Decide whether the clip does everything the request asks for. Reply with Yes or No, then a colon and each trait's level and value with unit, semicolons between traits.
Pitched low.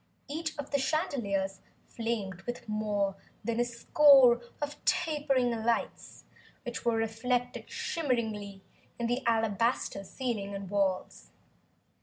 No: high, 235 Hz